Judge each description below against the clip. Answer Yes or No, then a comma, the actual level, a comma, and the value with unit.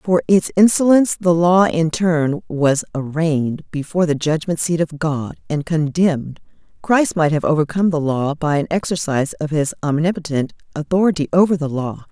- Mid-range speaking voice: Yes, medium, 160 Hz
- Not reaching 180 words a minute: Yes, average, 165 wpm